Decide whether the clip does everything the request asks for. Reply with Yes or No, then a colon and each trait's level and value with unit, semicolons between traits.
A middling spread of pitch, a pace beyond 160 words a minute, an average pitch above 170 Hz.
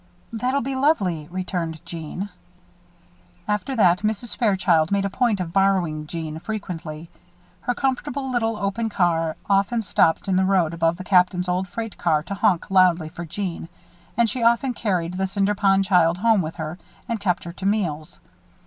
Yes: average, 4.2 semitones; average, 170 wpm; high, 190 Hz